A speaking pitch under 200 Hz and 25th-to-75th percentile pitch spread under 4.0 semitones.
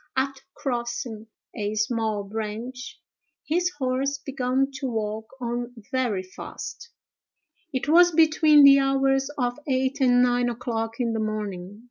No: high, 245 Hz; average, 3.4 semitones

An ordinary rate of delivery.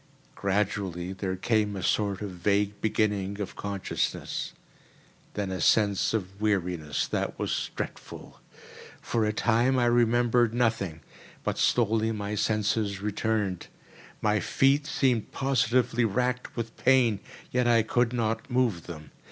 No: slow, 130 wpm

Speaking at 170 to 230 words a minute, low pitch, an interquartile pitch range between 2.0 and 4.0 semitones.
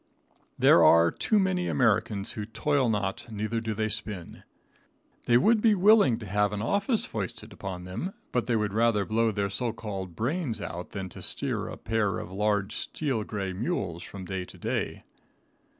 Yes: average, 180 wpm; low, 110 Hz; average, 3.5 semitones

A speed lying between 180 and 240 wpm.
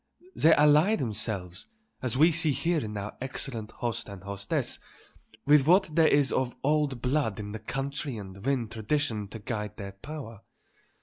No: average, 165 wpm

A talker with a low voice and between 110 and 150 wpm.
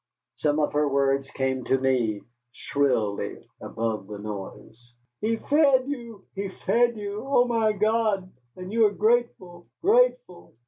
No: high, 190 Hz; average, 140 wpm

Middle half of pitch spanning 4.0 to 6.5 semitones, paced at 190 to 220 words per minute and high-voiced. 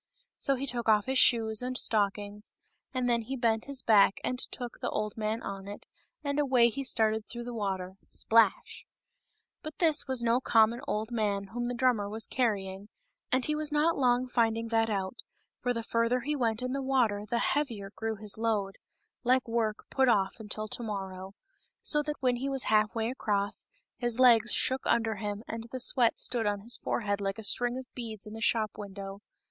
No: average, 3.2 semitones; fast, 205 wpm; high, 230 Hz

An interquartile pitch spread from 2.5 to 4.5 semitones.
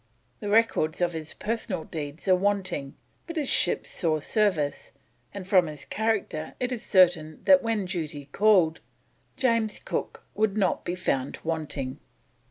No: wide, 5.6 semitones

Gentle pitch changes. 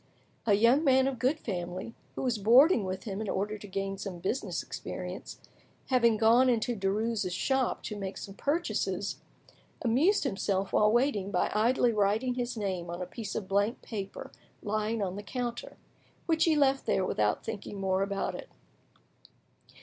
No: average, 4.2 semitones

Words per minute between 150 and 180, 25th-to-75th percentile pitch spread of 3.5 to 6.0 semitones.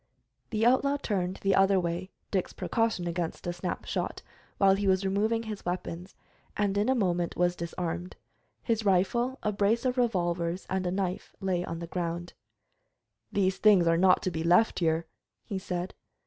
No: average, 175 wpm; average, 2.9 semitones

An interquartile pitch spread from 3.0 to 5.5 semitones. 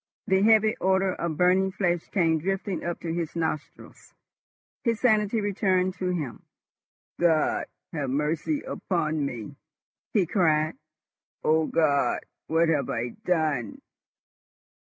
Yes: average, 3.7 semitones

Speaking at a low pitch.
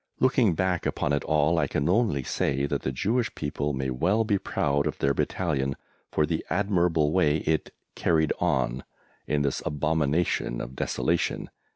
Yes: very low, 75 Hz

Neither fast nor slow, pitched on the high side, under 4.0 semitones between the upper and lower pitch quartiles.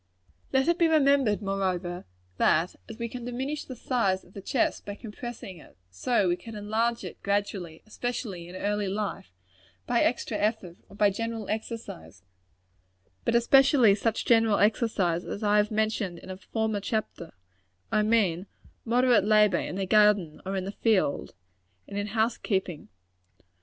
Yes: average, 160 wpm; high, 210 Hz; average, 3.3 semitones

